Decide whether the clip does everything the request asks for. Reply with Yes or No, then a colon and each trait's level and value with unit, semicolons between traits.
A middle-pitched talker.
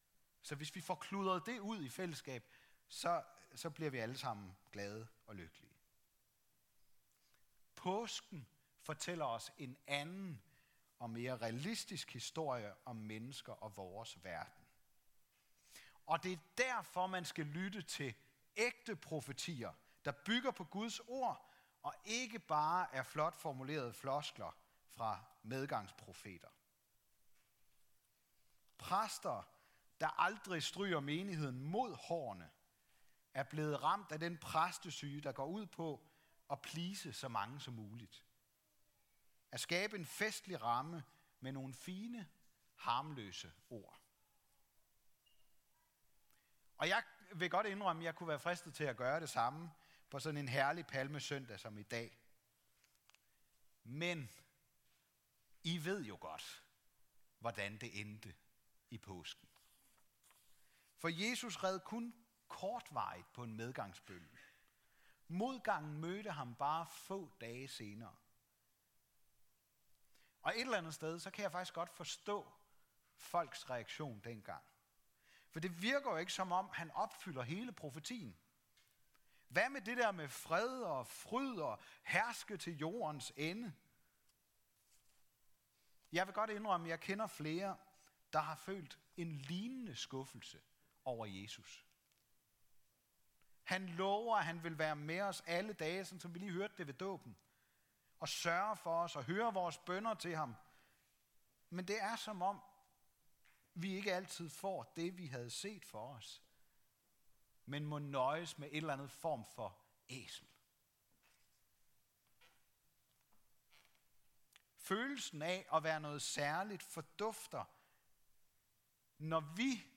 Yes: medium, 155 Hz